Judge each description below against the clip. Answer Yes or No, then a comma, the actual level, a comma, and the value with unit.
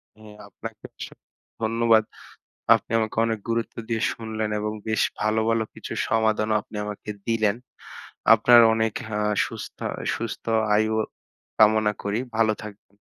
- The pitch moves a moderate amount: No, narrow, 0.9 semitones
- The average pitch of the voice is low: Yes, low, 110 Hz